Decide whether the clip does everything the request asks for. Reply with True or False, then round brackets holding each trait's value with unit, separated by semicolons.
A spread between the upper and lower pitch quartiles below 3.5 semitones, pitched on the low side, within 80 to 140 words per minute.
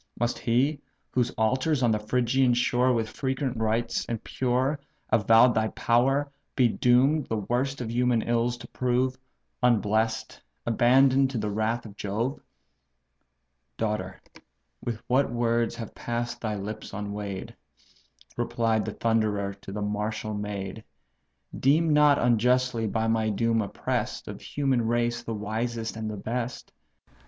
True (2.5 semitones; 115 Hz; 135 wpm)